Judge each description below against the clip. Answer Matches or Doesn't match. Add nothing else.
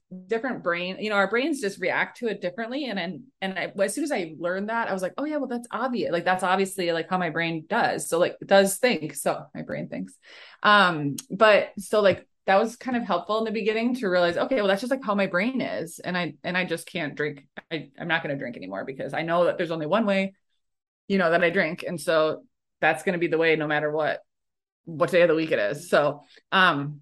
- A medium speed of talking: Doesn't match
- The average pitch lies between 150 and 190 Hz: Matches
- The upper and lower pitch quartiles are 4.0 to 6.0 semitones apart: Matches